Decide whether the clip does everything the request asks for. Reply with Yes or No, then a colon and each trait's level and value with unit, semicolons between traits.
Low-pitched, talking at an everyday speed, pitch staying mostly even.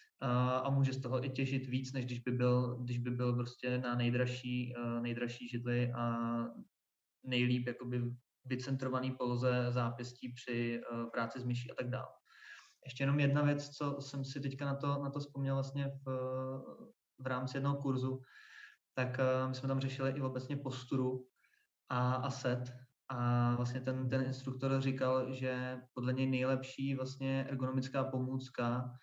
Yes: low, 130 Hz; average, 155 wpm; narrow, 1.4 semitones